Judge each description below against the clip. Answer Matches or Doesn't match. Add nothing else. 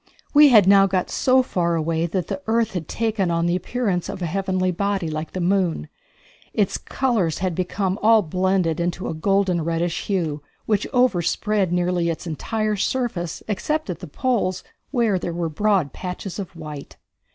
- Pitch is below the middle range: Doesn't match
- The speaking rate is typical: Matches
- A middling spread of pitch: Matches